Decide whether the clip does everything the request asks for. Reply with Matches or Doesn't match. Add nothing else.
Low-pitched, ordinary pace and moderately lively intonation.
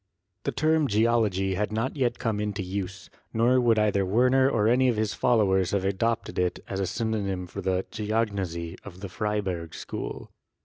Matches